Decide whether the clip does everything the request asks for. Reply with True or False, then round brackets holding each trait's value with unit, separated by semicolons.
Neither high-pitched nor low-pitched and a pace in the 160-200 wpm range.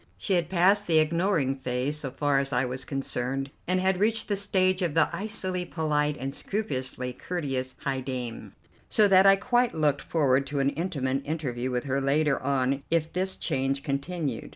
True (145 Hz; 180 wpm)